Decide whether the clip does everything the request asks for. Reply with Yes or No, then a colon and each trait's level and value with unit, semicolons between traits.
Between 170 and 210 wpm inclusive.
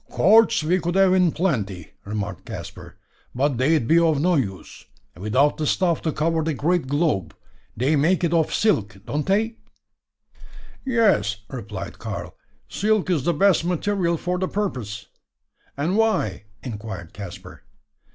No: average, 145 wpm